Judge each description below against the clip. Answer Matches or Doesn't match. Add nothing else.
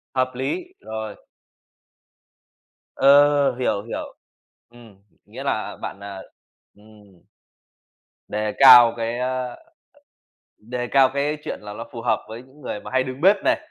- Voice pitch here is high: Doesn't match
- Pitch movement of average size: Matches